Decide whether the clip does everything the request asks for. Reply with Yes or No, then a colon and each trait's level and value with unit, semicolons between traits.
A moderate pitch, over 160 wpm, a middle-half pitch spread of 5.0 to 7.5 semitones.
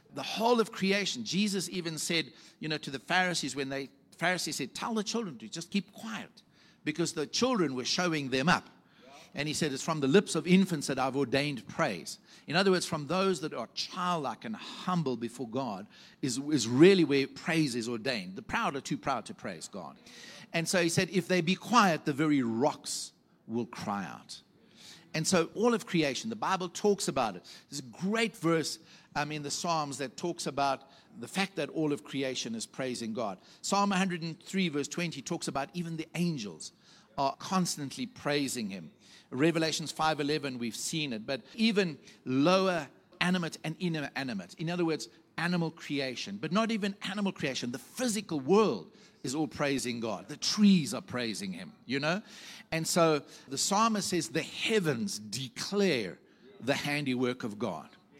Yes: medium, 165 Hz; average, 185 wpm; average, 5.3 semitones